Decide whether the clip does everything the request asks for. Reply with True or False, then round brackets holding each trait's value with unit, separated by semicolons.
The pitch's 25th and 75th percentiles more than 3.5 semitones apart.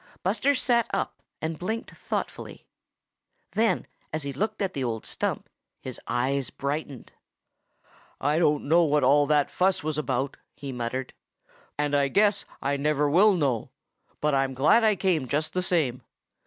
True (4.9 semitones)